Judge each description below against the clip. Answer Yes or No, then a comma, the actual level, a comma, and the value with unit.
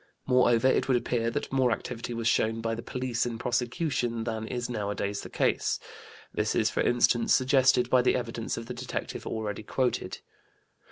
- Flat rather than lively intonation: Yes, narrow, 1.7 semitones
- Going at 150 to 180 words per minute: Yes, average, 175 wpm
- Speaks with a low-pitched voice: Yes, low, 120 Hz